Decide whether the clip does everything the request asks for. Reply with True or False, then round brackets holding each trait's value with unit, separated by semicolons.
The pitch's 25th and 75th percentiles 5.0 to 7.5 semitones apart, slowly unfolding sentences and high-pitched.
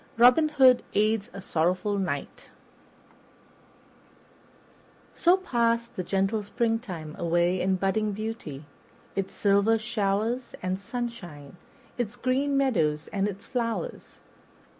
False (4.3 semitones; 105 wpm; 210 Hz)